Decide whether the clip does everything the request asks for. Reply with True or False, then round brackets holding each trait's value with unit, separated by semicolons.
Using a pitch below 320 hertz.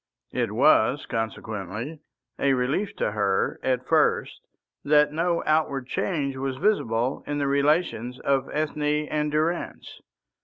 True (140 Hz)